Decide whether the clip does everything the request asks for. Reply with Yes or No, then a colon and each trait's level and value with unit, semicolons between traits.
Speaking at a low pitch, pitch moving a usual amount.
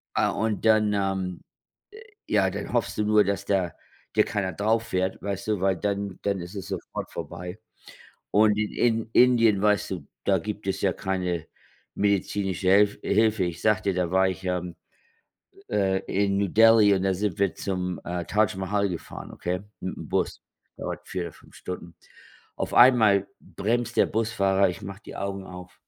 No: low, 100 Hz; narrow, 2.1 semitones